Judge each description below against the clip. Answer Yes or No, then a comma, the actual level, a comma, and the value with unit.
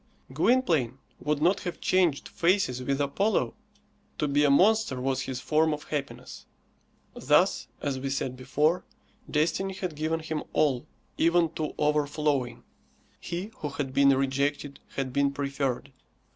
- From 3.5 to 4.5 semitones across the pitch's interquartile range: No, average, 3.1 semitones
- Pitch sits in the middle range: Yes, medium, 145 Hz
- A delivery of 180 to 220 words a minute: No, average, 140 wpm